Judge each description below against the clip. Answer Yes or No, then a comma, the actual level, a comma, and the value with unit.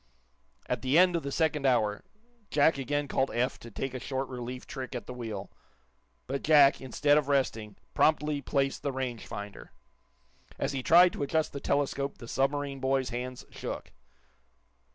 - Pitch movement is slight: Yes, narrow, 2.3 semitones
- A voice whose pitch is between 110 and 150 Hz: Yes, low, 135 Hz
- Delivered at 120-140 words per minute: No, average, 170 wpm